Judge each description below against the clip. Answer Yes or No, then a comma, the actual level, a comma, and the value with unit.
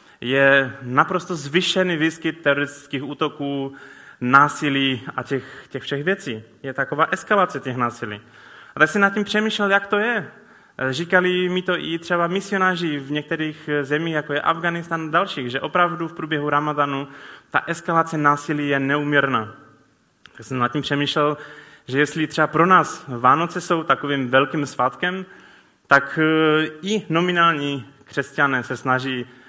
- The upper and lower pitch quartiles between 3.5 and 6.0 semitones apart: Yes, average, 3.8 semitones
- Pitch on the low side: No, medium, 150 Hz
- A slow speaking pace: No, average, 145 wpm